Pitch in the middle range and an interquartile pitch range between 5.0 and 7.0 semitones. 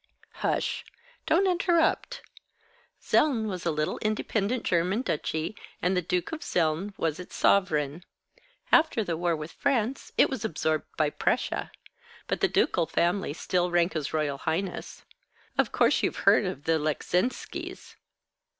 Yes: medium, 180 Hz; wide, 5.4 semitones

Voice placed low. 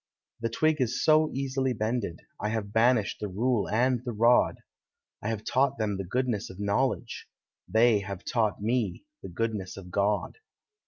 Yes: low, 115 Hz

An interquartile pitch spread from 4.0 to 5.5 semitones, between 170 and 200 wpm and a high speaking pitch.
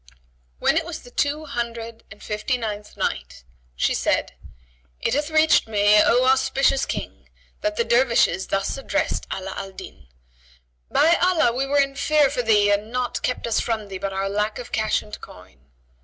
Yes: average, 4.9 semitones; average, 175 wpm; high, 235 Hz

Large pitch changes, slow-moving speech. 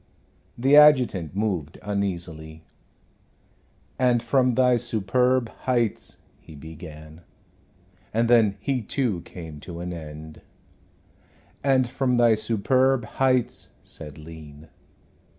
Yes: wide, 7.6 semitones; slow, 105 wpm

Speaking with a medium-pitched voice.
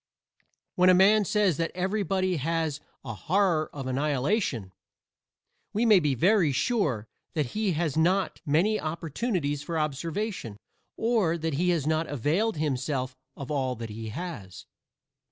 Yes: medium, 160 Hz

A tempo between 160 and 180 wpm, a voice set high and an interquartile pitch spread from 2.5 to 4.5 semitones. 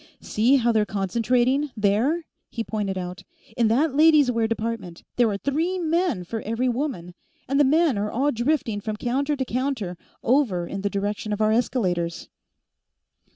No: average, 165 wpm; high, 230 Hz; average, 5.2 semitones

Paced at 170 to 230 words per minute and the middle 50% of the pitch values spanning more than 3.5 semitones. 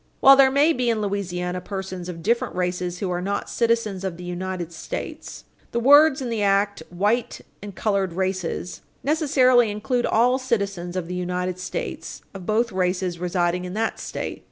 Yes: average, 175 wpm; average, 4.6 semitones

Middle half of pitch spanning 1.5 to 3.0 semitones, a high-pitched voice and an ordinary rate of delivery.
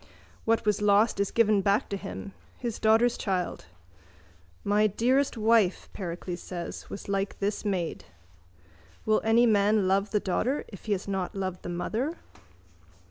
Yes: narrow, 2.6 semitones; high, 205 Hz; average, 150 wpm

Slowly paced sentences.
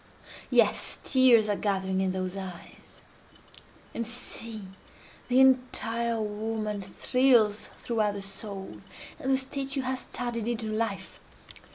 Yes: slow, 110 wpm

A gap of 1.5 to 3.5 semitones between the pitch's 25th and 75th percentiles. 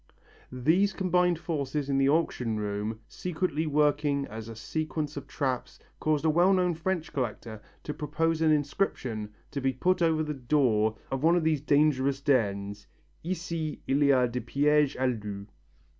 No: average, 4.2 semitones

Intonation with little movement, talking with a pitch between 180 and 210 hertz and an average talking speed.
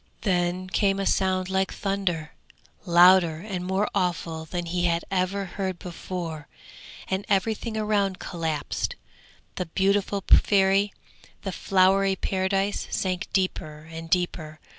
No: narrow, 2.0 semitones; medium, 185 Hz; slow, 125 wpm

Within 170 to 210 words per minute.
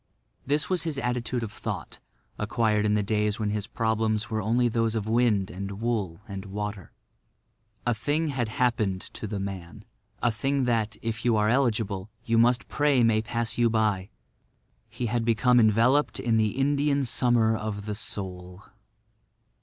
No: average, 160 wpm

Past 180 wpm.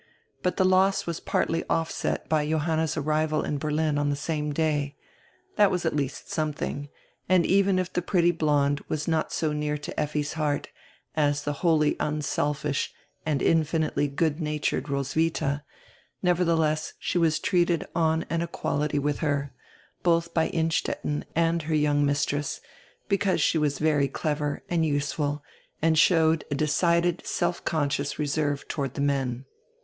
No: average, 155 wpm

